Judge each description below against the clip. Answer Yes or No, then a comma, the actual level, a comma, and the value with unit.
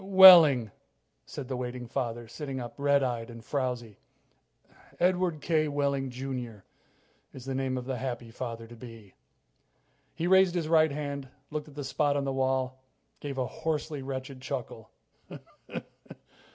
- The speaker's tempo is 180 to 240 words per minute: No, average, 150 wpm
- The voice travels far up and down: No, average, 3.2 semitones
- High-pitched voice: No, low, 135 Hz